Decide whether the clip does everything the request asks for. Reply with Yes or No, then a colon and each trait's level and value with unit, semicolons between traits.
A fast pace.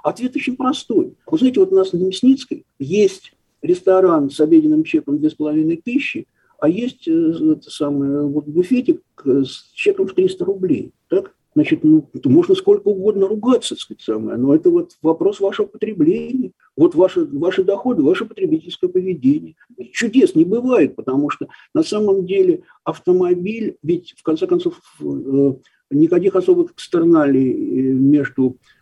No: average, 140 wpm